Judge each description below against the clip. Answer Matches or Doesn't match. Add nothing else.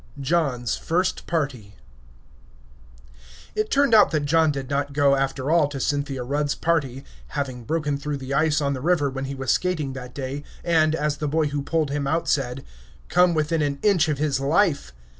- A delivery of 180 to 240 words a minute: Matches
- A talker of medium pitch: Matches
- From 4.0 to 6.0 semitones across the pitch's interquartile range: Doesn't match